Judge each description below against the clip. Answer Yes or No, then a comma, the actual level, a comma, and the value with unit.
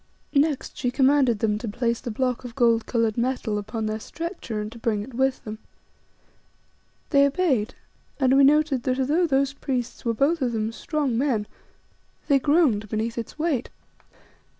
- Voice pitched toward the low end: No, very high, 250 Hz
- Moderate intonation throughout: Yes, average, 3.6 semitones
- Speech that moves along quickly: No, average, 170 wpm